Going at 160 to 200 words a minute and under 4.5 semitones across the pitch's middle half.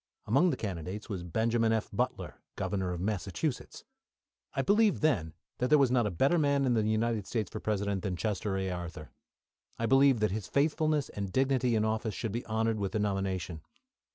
No: average, 185 wpm; average, 4.9 semitones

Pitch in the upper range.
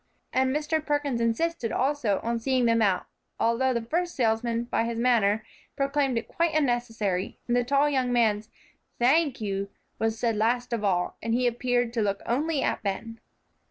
Yes: high, 240 Hz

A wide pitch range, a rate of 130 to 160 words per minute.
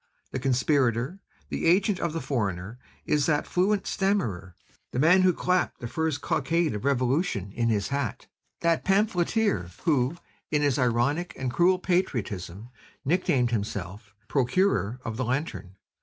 Yes: wide, 6.9 semitones; average, 145 wpm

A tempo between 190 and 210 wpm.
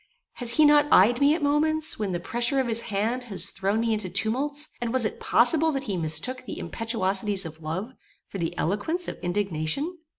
Yes: average, 200 wpm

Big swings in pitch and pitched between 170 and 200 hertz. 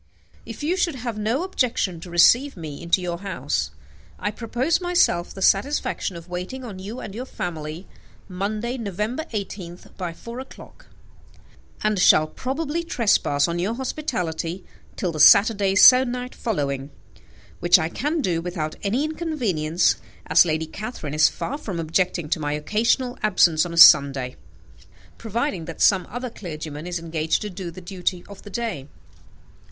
Yes: wide, 6.2 semitones; high, 190 Hz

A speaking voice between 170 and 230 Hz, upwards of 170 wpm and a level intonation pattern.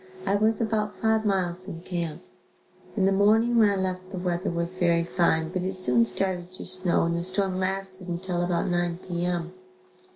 Yes: medium, 185 Hz; average, 195 wpm; narrow, 2.0 semitones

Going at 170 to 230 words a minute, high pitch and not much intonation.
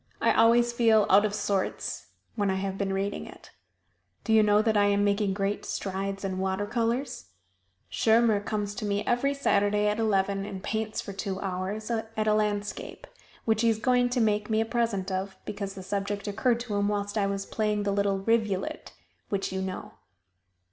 Yes: average, 190 wpm; high, 205 Hz; narrow, 2.0 semitones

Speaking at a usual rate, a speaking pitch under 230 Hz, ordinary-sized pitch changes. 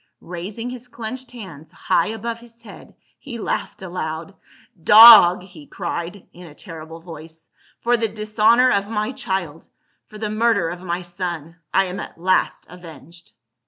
Yes: average, 175 wpm; high, 190 Hz; average, 4.9 semitones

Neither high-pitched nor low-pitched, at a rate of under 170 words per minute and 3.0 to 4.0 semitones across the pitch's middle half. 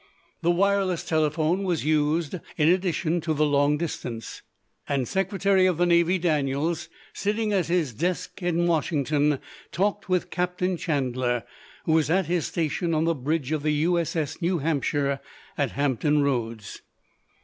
Yes: medium, 160 Hz; average, 150 wpm; average, 3.5 semitones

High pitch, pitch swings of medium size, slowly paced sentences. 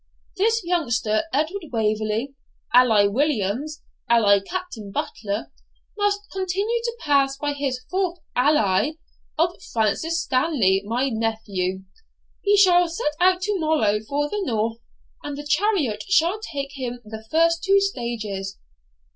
No: very high, 280 Hz; wide, 8.2 semitones; slow, 130 wpm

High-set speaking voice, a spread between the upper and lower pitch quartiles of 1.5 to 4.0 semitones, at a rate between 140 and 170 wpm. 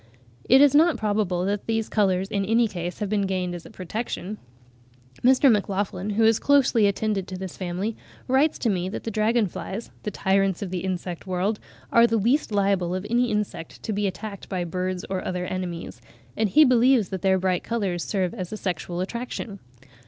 No: high, 200 Hz; average, 3.4 semitones; average, 185 wpm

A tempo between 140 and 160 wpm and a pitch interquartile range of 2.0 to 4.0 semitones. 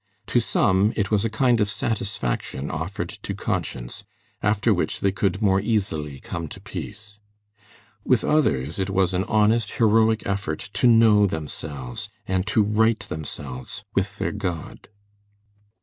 No: average, 145 wpm; average, 4.5 semitones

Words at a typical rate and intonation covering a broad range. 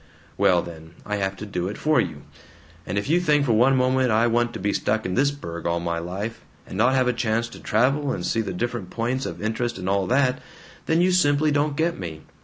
No: fast, 240 wpm; wide, 5.9 semitones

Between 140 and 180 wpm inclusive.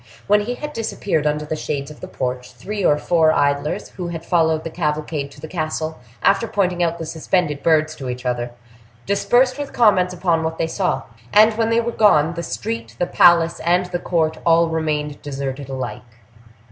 No: average, 195 wpm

